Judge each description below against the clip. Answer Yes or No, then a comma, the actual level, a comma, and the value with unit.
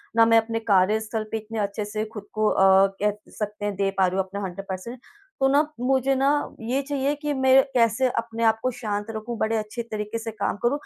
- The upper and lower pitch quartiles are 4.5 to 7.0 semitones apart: No, average, 2.9 semitones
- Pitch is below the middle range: No, high, 220 Hz